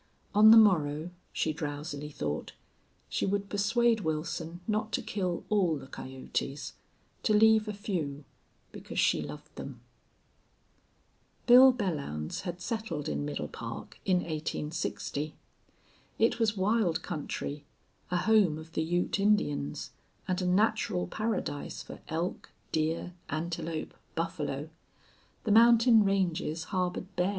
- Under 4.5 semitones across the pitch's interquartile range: No, wide, 5.5 semitones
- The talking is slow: Yes, slow, 125 wpm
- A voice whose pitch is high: No, medium, 175 Hz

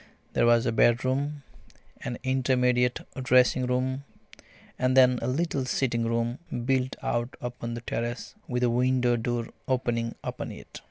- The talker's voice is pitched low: Yes, low, 125 Hz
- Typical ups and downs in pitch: No, narrow, 1.6 semitones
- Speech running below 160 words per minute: Yes, average, 145 wpm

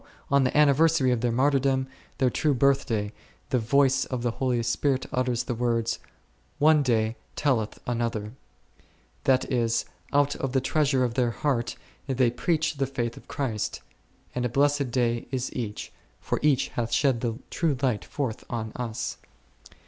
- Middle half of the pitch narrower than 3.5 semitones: Yes, average, 2.8 semitones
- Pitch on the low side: Yes, low, 125 Hz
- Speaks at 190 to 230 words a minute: No, average, 165 wpm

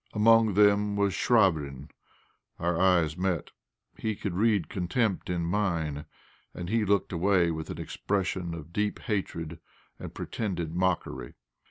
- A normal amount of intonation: Yes, average, 3.5 semitones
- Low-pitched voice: Yes, very low, 95 Hz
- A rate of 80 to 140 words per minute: Yes, slow, 135 wpm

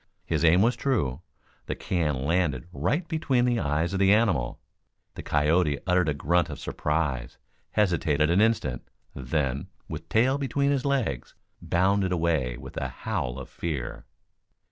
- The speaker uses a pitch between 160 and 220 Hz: No, very low, 85 Hz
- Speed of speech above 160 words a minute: No, average, 150 wpm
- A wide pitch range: Yes, wide, 6.8 semitones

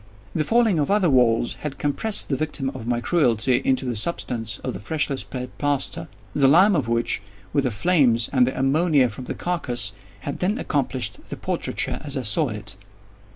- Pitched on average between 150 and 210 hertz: No, low, 135 Hz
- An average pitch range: Yes, average, 4.5 semitones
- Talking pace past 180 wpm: Yes, average, 190 wpm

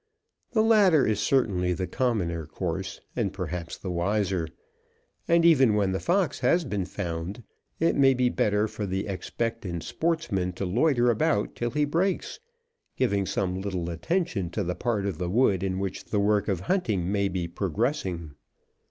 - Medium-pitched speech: No, low, 100 Hz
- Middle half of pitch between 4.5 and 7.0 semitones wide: Yes, wide, 5.5 semitones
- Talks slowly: No, average, 165 wpm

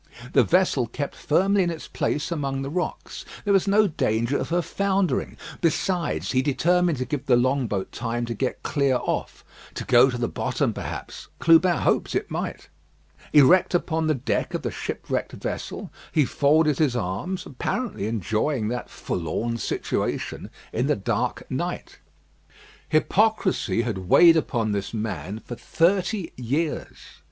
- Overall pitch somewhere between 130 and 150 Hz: Yes, medium, 140 Hz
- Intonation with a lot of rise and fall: Yes, wide, 6.5 semitones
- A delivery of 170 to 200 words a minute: No, average, 155 wpm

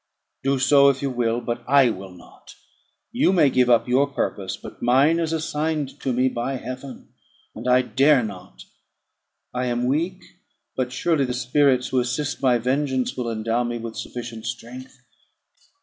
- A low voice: Yes, low, 130 Hz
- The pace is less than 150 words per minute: No, average, 165 wpm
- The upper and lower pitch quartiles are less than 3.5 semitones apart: Yes, narrow, 2.6 semitones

